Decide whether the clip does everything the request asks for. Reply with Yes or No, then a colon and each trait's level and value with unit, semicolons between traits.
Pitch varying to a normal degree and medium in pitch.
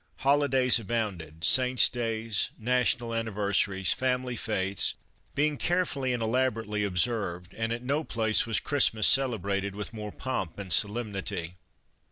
No: average, 3.9 semitones; low, 115 Hz